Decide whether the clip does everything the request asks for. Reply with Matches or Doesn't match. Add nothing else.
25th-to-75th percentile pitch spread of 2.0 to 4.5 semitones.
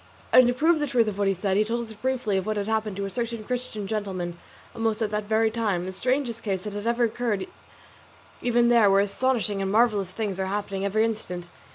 Matches